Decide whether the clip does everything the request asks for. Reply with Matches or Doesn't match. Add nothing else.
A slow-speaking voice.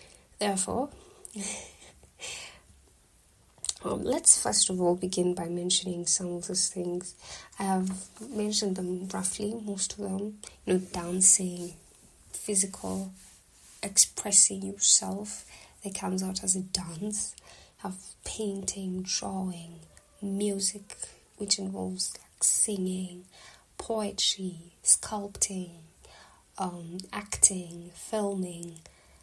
Matches